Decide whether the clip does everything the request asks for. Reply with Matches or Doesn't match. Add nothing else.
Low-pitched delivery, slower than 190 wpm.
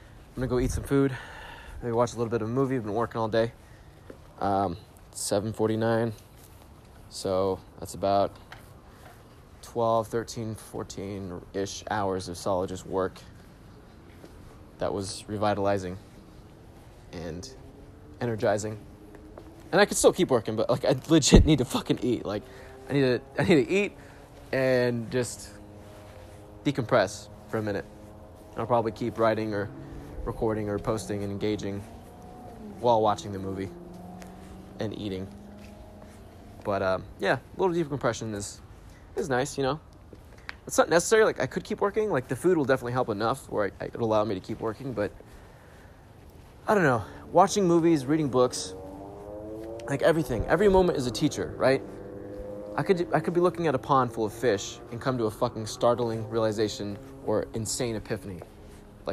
Matches